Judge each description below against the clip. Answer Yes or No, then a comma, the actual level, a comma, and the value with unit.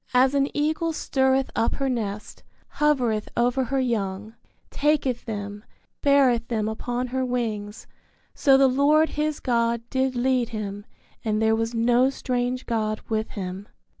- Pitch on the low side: No, high, 245 Hz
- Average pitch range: Yes, average, 3.4 semitones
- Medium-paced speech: Yes, average, 145 wpm